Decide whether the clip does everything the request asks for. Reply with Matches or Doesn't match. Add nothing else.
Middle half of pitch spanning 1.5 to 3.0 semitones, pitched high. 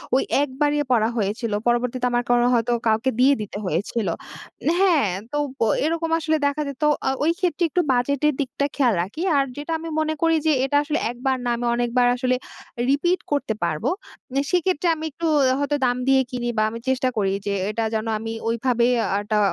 Doesn't match